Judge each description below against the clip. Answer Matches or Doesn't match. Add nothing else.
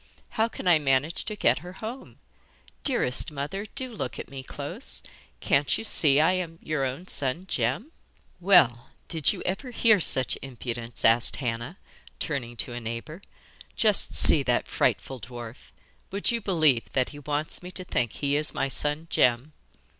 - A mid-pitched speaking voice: Matches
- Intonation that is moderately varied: Doesn't match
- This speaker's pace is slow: Doesn't match